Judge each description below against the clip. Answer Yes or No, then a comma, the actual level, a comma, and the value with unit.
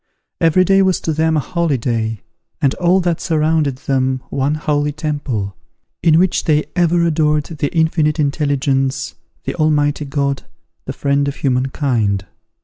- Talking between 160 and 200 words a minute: No, average, 145 wpm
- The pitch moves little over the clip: No, average, 3.0 semitones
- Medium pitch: Yes, medium, 150 Hz